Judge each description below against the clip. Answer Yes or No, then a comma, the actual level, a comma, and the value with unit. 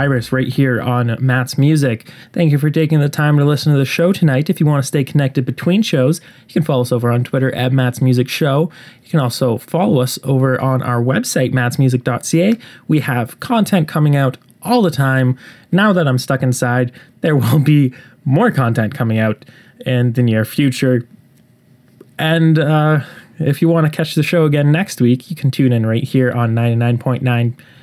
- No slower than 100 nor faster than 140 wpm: No, average, 195 wpm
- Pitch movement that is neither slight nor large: Yes, average, 3.7 semitones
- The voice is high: No, low, 135 Hz